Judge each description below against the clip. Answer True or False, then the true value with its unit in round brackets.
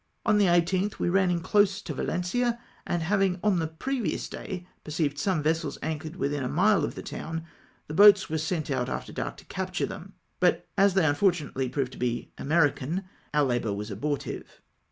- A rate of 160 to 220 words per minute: True (195 wpm)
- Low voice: False (165 Hz)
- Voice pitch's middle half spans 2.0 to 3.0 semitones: False (4.8 semitones)